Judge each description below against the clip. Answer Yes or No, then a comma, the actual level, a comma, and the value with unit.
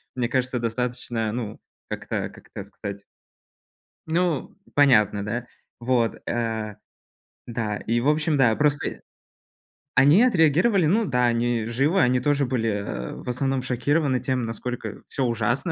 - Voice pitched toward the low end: Yes, low, 125 Hz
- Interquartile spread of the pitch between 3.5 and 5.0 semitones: Yes, average, 4.0 semitones